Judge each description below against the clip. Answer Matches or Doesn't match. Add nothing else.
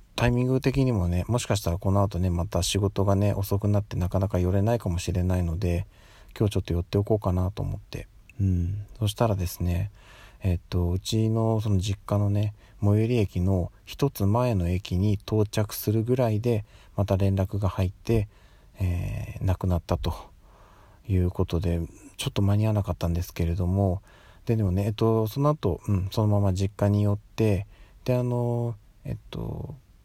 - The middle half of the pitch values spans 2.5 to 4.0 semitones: Matches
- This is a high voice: Doesn't match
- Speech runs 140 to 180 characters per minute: Doesn't match